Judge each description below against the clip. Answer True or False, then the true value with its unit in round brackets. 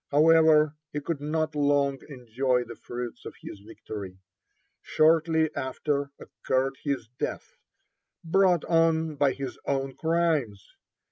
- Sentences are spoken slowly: True (120 wpm)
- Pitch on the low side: False (145 Hz)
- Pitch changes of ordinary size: True (3.6 semitones)